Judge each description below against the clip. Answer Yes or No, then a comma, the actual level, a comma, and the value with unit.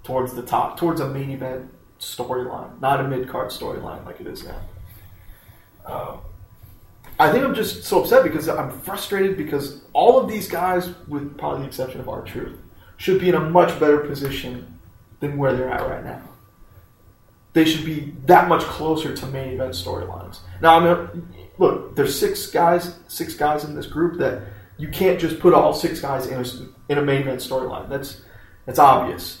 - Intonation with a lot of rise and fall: Yes, wide, 6.4 semitones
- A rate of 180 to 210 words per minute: Yes, average, 185 wpm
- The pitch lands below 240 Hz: Yes, low, 135 Hz